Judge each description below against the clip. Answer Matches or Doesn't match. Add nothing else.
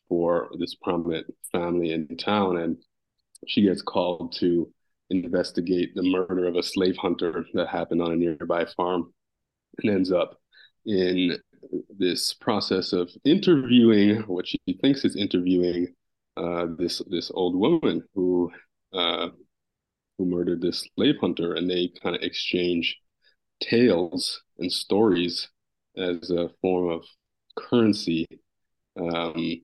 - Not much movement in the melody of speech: Matches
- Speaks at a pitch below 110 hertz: Matches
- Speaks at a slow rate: Matches